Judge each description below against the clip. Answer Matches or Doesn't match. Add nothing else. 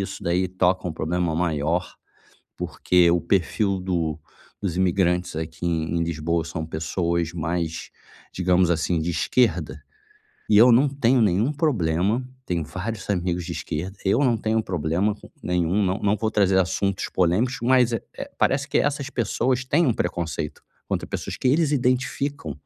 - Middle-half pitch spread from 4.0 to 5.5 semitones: Matches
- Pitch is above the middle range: Doesn't match